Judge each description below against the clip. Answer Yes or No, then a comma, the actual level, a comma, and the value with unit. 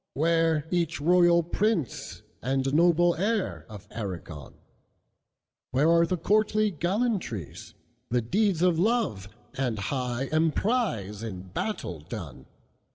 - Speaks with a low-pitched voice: No, medium, 165 Hz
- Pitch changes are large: Yes, wide, 7.5 semitones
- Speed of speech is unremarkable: No, slow, 90 wpm